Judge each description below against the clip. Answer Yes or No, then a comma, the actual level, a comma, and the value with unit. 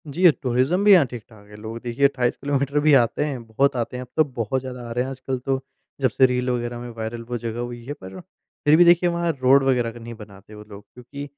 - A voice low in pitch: Yes, low, 125 Hz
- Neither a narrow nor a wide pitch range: Yes, average, 3.1 semitones